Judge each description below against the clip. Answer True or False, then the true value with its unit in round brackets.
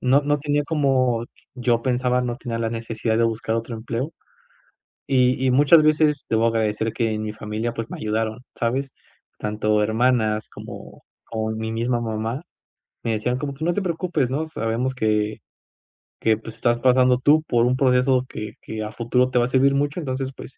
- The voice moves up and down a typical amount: True (3.0 semitones)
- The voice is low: True (120 Hz)